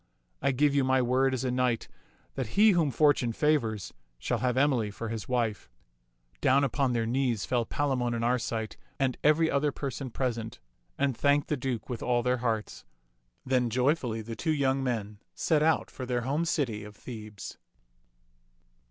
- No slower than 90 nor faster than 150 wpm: No, average, 170 wpm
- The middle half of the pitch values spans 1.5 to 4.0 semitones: Yes, average, 3.3 semitones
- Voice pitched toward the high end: No, low, 125 Hz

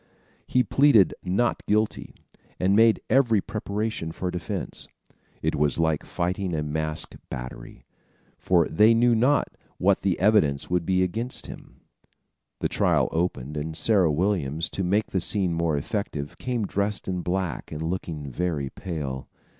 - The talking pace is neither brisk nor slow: Yes, average, 145 wpm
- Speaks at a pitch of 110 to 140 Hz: No, very low, 90 Hz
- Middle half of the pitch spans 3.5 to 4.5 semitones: No, average, 5.0 semitones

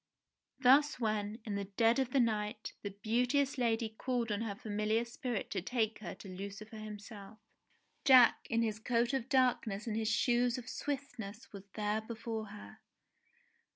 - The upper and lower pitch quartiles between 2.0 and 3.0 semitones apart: Yes, average, 2.7 semitones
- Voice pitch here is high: Yes, high, 225 Hz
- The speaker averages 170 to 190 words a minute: No, average, 160 wpm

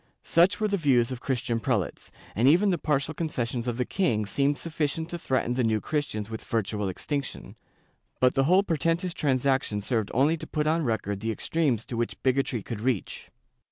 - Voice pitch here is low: Yes, low, 130 Hz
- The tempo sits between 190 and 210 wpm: Yes, average, 200 wpm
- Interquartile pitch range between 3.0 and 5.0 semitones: No, wide, 5.5 semitones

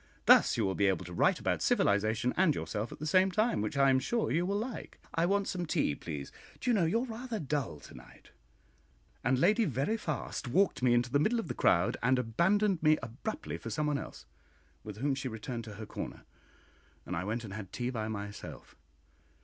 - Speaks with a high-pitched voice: No, low, 130 Hz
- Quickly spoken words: Yes, fast, 215 wpm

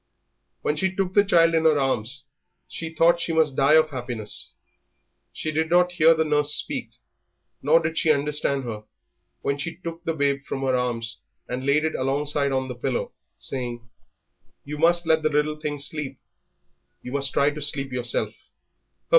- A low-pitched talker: No, medium, 150 Hz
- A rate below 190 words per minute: Yes, average, 175 wpm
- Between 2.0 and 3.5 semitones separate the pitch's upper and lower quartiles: Yes, average, 3.1 semitones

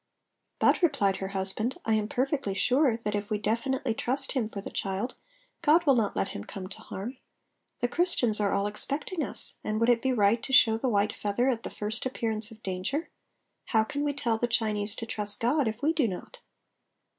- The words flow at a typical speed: No, fast, 210 wpm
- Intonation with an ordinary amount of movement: Yes, average, 4.2 semitones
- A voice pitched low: No, high, 225 Hz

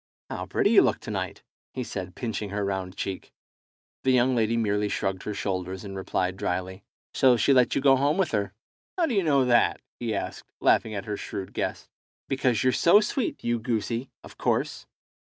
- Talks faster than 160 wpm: Yes, average, 195 wpm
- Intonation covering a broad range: No, average, 4.9 semitones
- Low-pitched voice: Yes, low, 110 Hz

